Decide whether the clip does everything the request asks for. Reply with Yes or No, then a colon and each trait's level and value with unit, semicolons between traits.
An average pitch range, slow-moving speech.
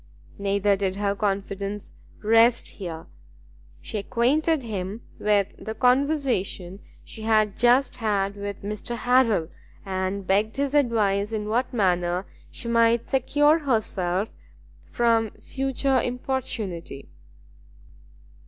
Yes: average, 3.8 semitones; slow, 105 wpm